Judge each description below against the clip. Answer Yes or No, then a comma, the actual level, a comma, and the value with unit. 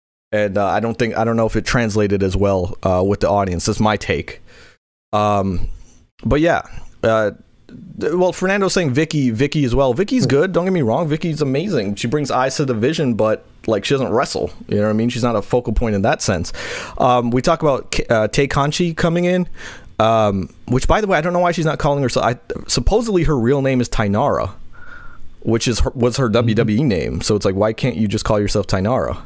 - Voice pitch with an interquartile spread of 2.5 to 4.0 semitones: No, wide, 5.4 semitones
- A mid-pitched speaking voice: No, low, 120 Hz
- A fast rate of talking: Yes, fast, 220 wpm